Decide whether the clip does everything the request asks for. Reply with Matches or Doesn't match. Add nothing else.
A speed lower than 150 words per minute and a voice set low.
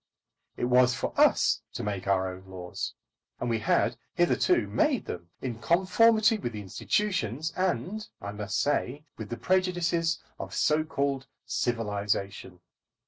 Matches